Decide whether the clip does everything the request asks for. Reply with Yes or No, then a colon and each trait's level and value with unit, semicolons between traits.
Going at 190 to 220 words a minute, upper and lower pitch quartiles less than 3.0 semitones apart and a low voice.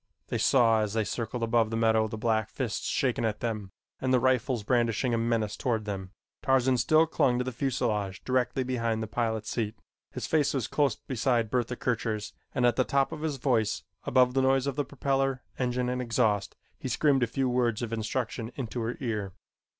Yes: average, 195 wpm; narrow, 2.6 semitones; low, 120 Hz